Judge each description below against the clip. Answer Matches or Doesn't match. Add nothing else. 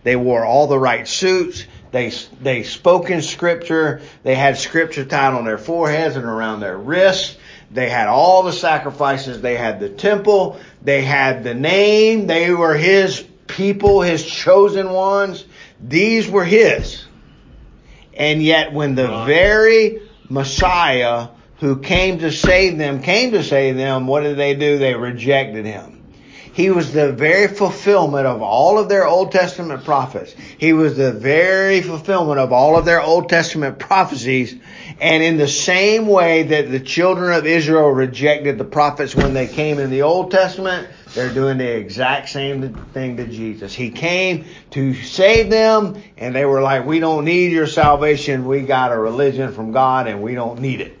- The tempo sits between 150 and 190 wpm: Matches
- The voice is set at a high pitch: Doesn't match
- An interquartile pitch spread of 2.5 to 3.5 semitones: Doesn't match